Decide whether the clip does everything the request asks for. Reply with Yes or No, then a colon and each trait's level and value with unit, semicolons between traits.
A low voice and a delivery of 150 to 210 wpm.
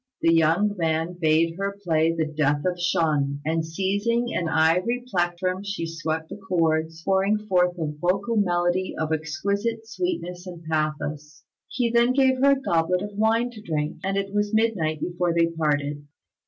No: medium, 175 Hz; average, 170 wpm